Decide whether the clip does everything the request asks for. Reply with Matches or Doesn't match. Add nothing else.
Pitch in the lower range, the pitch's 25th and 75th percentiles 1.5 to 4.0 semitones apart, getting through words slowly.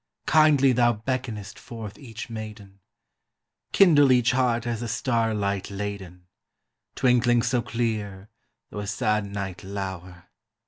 Matches